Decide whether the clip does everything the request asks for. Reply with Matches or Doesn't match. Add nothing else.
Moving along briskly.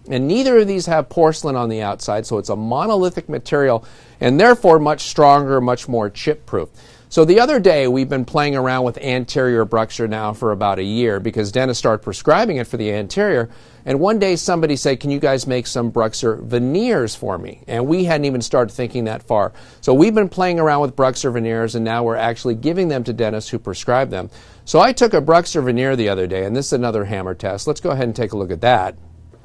Matches